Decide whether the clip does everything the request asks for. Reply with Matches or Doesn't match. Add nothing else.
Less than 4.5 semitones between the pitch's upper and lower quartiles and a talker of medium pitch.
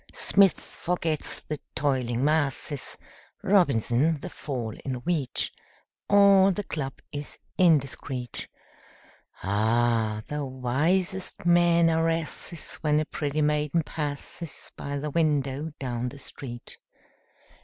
Matches